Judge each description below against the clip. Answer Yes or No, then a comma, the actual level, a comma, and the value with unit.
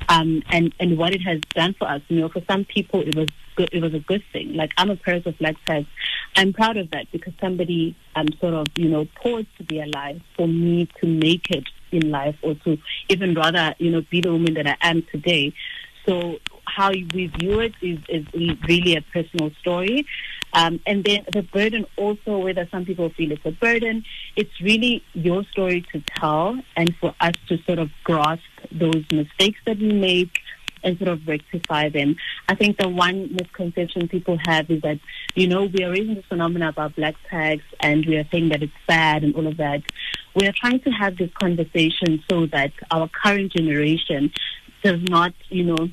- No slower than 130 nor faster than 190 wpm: No, fast, 205 wpm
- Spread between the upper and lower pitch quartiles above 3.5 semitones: No, average, 3.2 semitones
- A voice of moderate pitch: Yes, medium, 170 Hz